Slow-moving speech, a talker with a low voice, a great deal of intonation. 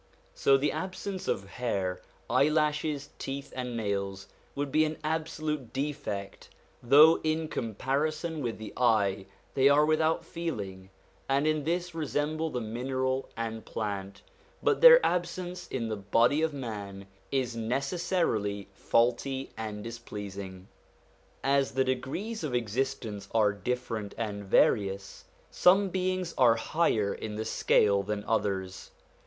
Yes: slow, 130 wpm; low, 130 Hz; wide, 6.7 semitones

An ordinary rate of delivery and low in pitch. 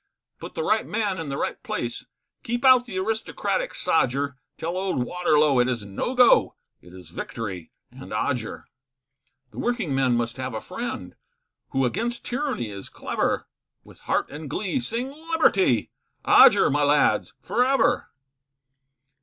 No: average, 150 wpm; medium, 165 Hz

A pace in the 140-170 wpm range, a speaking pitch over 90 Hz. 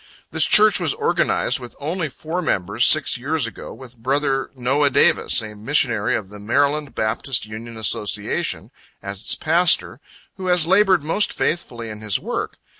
Yes: average, 160 wpm; low, 135 Hz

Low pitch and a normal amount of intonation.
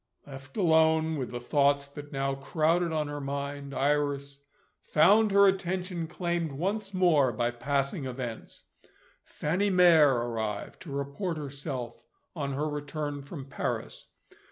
No: medium, 145 Hz; average, 3.5 semitones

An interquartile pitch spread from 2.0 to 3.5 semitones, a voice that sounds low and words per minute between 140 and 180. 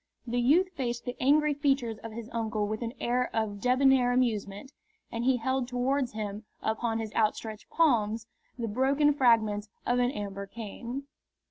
No: average, 3.1 semitones; high, 240 Hz; average, 160 wpm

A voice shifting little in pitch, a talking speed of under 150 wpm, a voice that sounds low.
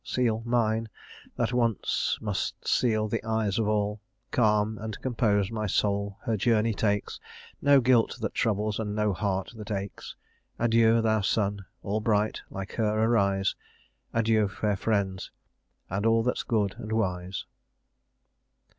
Yes: narrow, 1.9 semitones; average, 140 wpm; low, 110 Hz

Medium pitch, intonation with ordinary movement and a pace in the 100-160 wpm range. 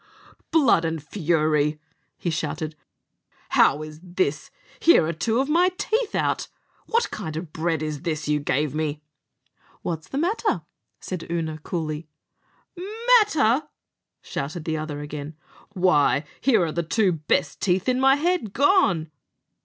No: medium, 165 Hz; wide, 8.9 semitones; average, 140 wpm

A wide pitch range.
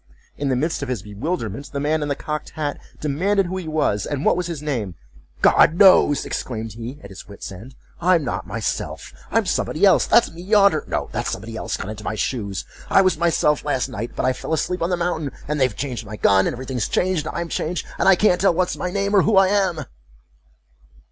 Yes: wide, 7.4 semitones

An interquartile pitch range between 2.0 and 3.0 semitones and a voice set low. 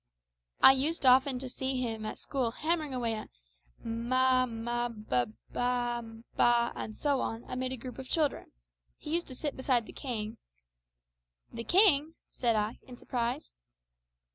No: narrow, 2.6 semitones; high, 245 Hz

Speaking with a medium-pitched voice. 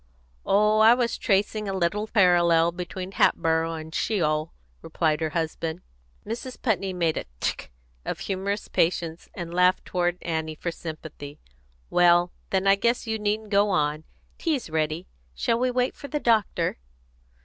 Yes: medium, 180 Hz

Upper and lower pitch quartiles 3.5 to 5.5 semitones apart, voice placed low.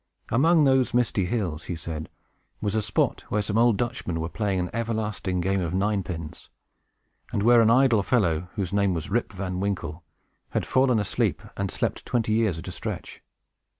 Yes: average, 4.3 semitones; low, 100 Hz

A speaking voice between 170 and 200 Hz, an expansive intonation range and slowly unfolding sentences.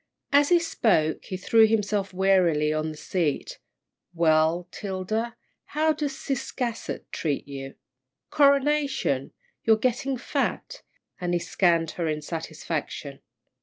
Yes: high, 190 Hz; wide, 8.1 semitones; slow, 120 wpm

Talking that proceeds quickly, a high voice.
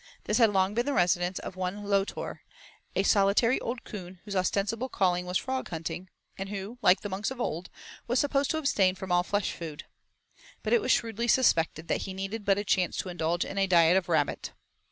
Yes: fast, 210 wpm; high, 195 Hz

